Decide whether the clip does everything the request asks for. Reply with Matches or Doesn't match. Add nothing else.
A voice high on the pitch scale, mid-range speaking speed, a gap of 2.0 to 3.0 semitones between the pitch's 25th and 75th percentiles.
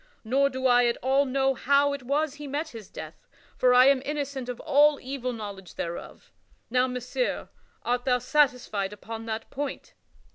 Matches